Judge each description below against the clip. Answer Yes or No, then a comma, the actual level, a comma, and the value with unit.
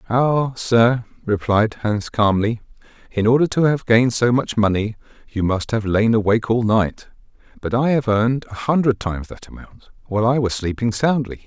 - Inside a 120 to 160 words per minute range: No, average, 180 wpm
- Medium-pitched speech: No, low, 115 Hz